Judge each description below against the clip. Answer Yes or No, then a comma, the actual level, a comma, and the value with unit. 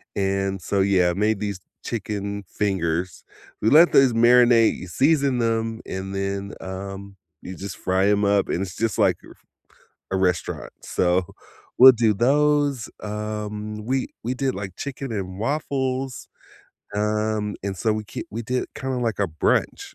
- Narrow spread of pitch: No, average, 3.8 semitones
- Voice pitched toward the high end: No, low, 105 Hz